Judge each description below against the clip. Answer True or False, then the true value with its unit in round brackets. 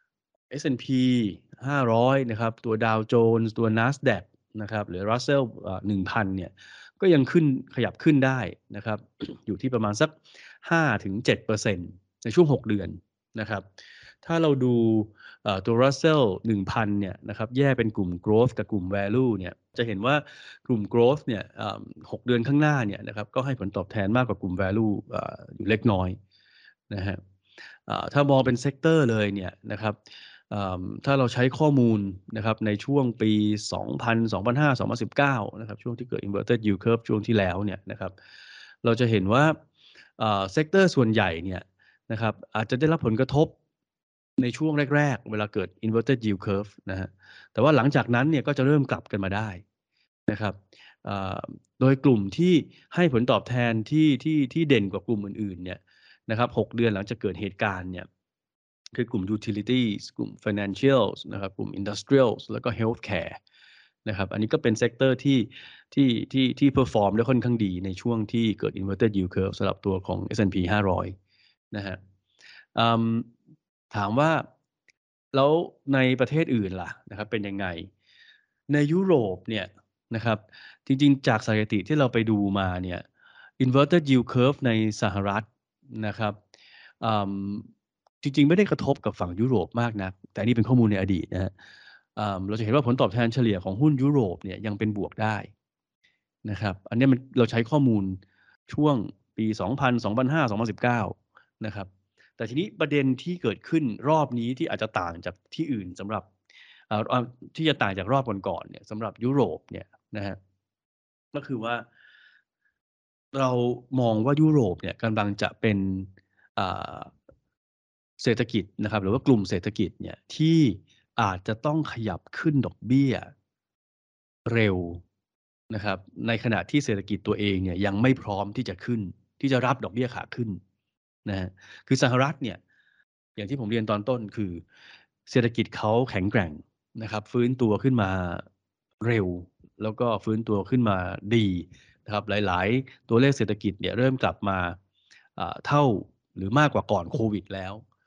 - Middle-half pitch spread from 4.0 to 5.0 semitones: True (4.3 semitones)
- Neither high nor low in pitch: False (110 Hz)